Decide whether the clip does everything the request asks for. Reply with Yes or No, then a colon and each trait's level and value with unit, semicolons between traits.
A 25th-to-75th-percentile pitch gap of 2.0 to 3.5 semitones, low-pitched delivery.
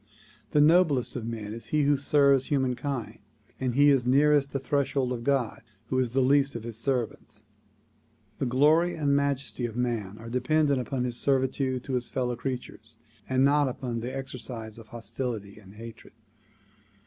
Yes: average, 2.9 semitones; low, 130 Hz